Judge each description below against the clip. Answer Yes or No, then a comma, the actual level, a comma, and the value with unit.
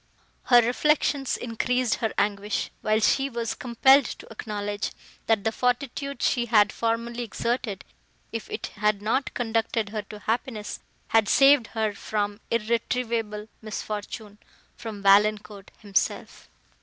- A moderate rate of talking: No, slow, 120 wpm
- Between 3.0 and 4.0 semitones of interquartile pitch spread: No, narrow, 2.4 semitones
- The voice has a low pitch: No, high, 225 Hz